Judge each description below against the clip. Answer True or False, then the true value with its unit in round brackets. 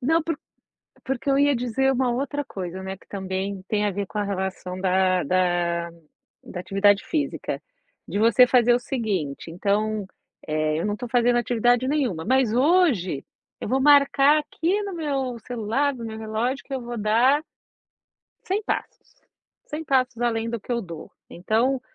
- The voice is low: False (235 Hz)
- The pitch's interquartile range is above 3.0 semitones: True (5.6 semitones)